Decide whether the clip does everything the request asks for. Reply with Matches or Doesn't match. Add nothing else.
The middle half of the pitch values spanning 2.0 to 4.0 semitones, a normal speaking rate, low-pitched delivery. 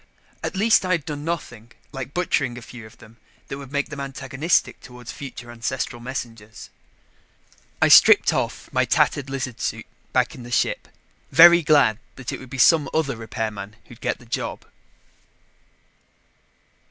Matches